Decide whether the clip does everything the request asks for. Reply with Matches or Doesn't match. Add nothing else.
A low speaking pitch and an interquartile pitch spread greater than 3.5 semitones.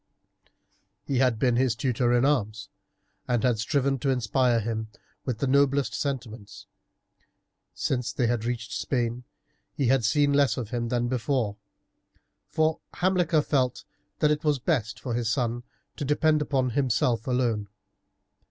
Doesn't match